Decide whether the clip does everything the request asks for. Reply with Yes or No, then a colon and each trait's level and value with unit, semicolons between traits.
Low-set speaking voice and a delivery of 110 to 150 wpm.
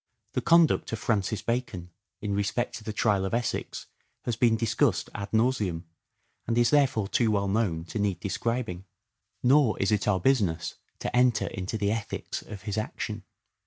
No: low, 110 Hz; average, 175 wpm